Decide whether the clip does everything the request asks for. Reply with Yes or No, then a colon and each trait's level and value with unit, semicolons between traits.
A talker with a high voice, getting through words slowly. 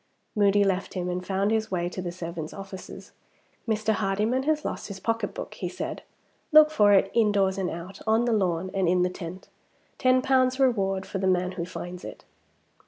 No: high, 195 Hz; average, 190 wpm